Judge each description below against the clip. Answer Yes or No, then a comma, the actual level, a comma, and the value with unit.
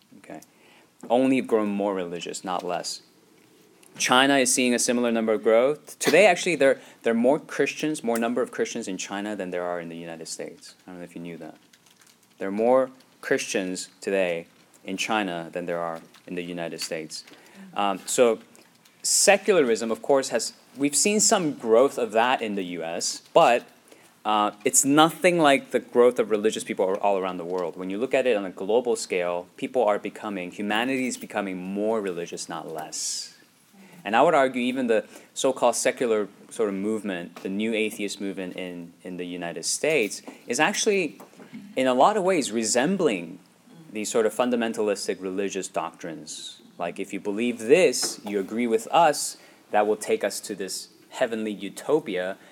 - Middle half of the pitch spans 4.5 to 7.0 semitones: Yes, average, 5.2 semitones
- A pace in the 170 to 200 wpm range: Yes, average, 180 wpm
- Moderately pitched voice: No, low, 105 Hz